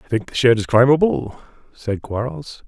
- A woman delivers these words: No, male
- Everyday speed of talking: Yes, average, 180 wpm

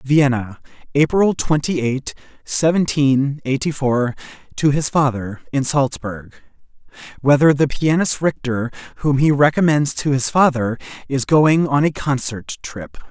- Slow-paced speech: Yes, slow, 130 wpm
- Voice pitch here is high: No, medium, 140 Hz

